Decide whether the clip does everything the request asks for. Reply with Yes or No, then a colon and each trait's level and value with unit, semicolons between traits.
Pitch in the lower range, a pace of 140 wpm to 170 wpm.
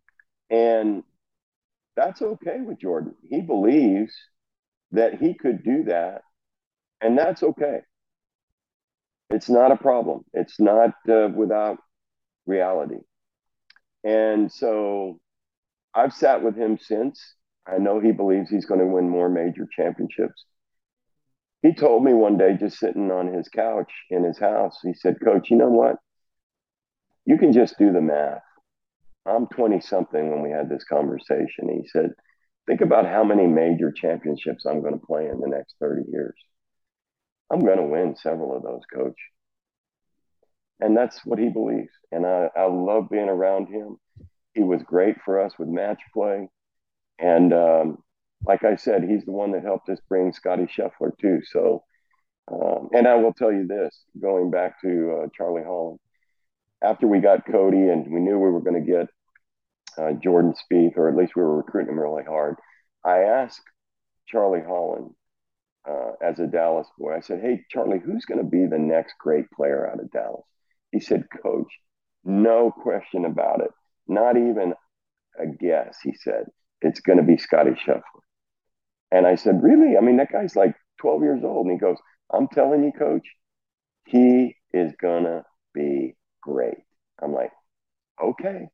Yes: very low, 95 Hz; average, 165 wpm